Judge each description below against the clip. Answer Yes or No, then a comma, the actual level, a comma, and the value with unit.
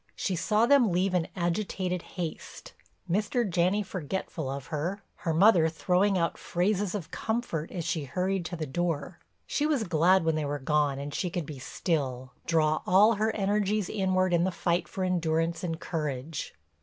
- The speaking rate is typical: Yes, average, 175 wpm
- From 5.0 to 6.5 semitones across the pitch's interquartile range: No, average, 3.4 semitones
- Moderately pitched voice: Yes, medium, 175 Hz